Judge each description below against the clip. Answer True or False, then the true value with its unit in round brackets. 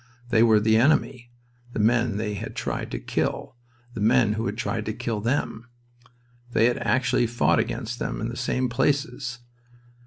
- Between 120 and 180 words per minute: True (175 wpm)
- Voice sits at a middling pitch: False (115 Hz)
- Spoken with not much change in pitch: True (2.0 semitones)